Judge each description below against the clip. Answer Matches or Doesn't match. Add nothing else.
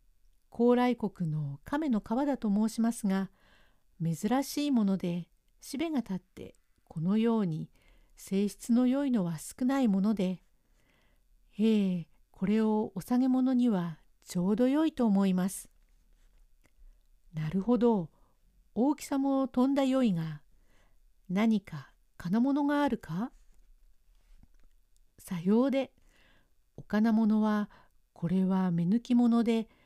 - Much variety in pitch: Matches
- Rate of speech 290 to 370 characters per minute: Doesn't match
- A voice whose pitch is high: Matches